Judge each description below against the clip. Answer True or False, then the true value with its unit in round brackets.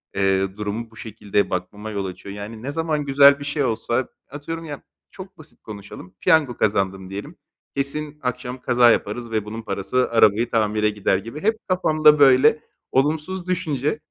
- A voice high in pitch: False (120 Hz)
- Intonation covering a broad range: True (6.3 semitones)